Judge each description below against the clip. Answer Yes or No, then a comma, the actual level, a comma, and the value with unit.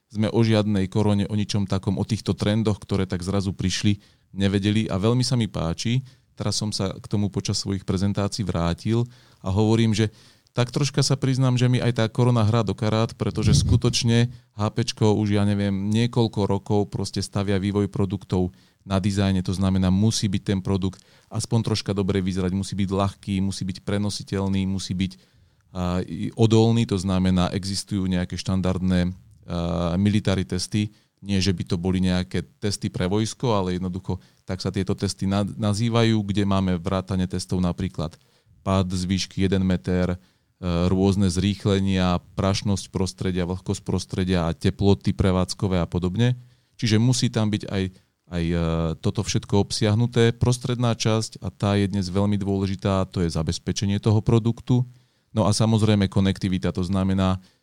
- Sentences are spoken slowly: No, average, 155 wpm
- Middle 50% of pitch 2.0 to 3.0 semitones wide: Yes, average, 2.7 semitones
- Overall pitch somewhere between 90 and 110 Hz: Yes, low, 100 Hz